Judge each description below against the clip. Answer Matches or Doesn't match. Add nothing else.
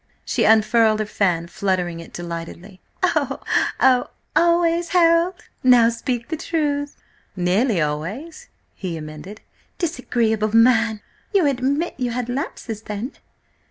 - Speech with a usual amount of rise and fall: Doesn't match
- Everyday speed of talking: Doesn't match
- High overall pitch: Matches